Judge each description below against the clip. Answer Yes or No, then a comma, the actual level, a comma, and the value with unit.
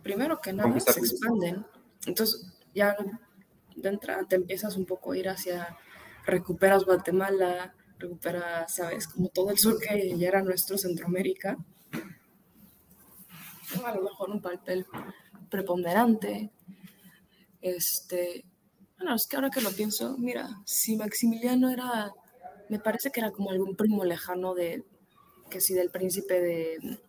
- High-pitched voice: Yes, high, 195 Hz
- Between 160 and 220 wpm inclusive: No, average, 135 wpm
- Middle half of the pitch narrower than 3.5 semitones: Yes, average, 2.8 semitones